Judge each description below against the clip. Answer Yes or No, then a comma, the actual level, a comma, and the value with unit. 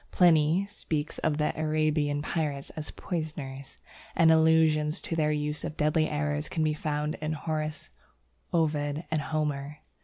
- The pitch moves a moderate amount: No, narrow, 1.1 semitones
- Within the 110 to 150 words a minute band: Yes, average, 145 wpm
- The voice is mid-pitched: Yes, medium, 155 Hz